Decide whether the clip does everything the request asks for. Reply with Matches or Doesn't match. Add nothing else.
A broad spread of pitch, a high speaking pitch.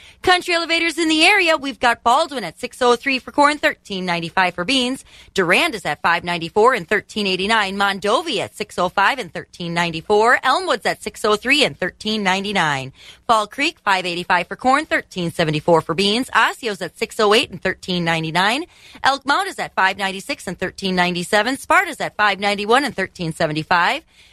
Matches